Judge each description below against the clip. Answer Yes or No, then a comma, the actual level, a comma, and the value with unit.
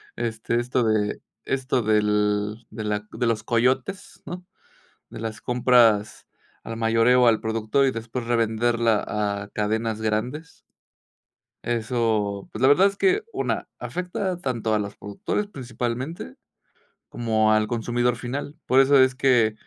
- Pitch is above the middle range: No, low, 115 Hz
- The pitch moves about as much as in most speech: Yes, average, 3.0 semitones